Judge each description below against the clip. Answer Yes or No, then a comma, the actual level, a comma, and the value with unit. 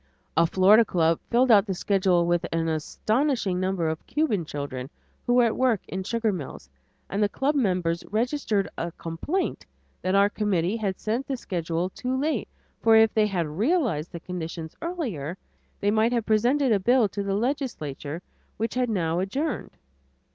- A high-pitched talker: Yes, high, 200 Hz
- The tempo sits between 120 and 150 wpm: No, average, 170 wpm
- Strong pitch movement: Yes, wide, 5.7 semitones